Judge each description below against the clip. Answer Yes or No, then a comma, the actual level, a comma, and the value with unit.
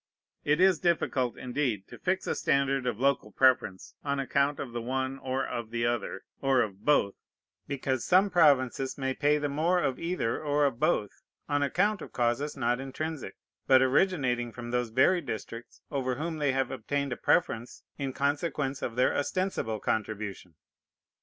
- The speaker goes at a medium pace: Yes, average, 170 wpm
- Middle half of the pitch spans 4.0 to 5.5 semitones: No, average, 3.5 semitones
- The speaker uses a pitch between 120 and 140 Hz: Yes, low, 135 Hz